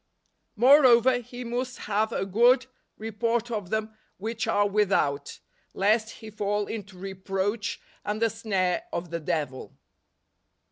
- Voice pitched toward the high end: Yes, high, 215 Hz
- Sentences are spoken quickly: No, slow, 135 wpm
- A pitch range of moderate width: Yes, average, 3.1 semitones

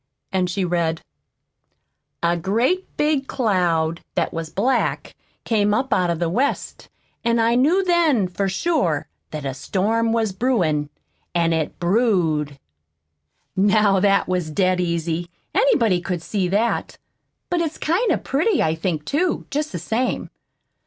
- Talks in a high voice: Yes, high, 195 Hz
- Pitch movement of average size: No, wide, 6.7 semitones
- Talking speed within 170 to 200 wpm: No, average, 145 wpm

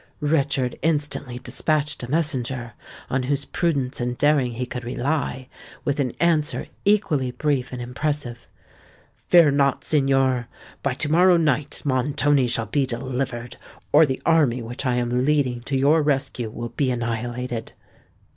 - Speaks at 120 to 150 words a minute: Yes, average, 145 wpm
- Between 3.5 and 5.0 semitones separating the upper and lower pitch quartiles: No, average, 3.1 semitones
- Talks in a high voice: No, low, 135 Hz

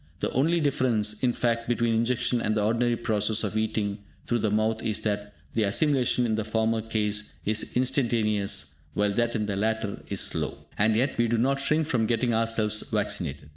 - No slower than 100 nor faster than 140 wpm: No, average, 190 wpm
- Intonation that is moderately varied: No, narrow, 2.0 semitones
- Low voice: Yes, low, 110 Hz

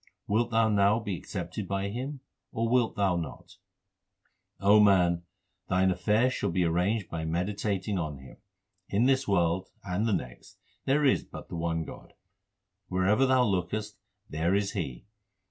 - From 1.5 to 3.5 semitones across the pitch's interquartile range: No, average, 4.1 semitones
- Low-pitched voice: Yes, low, 100 Hz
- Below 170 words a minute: Yes, average, 155 wpm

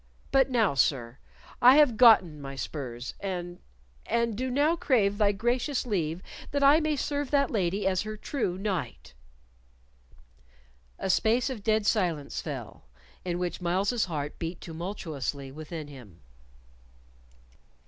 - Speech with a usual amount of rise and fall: No, wide, 7.2 semitones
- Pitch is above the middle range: Yes, high, 195 Hz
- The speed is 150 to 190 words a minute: No, slow, 135 wpm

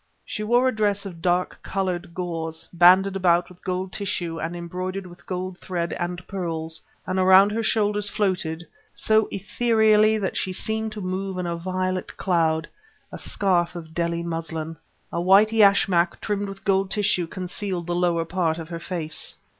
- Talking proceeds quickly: No, average, 170 wpm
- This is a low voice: No, medium, 185 Hz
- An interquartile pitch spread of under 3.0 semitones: Yes, narrow, 2.5 semitones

